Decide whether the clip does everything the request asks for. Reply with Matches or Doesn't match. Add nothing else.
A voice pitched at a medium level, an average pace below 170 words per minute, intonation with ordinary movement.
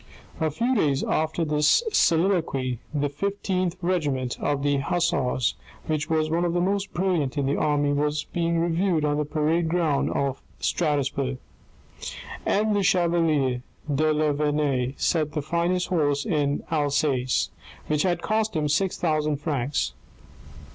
Matches